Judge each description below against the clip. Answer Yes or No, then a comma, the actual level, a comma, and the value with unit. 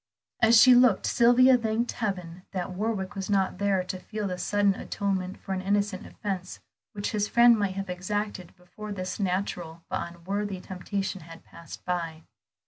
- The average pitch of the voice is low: No, high, 195 Hz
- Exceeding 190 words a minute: No, average, 165 wpm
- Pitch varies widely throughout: No, narrow, 2.4 semitones